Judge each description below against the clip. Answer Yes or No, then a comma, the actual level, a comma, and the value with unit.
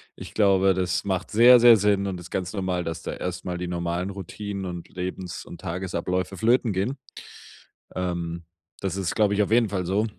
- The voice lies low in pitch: Yes, very low, 95 Hz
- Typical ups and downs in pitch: No, narrow, 2.3 semitones